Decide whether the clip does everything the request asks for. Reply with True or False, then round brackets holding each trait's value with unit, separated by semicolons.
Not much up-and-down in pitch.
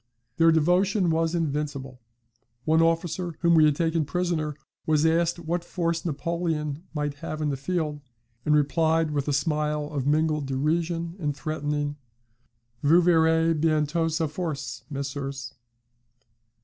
True (2.1 semitones)